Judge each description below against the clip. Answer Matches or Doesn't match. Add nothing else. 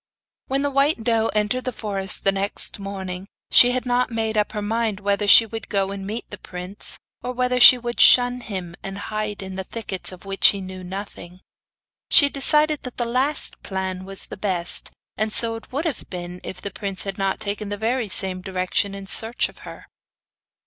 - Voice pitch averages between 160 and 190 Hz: Doesn't match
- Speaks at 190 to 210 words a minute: Matches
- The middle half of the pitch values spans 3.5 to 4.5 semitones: Matches